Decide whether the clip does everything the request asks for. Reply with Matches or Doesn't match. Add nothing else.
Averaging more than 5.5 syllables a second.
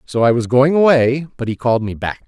Matches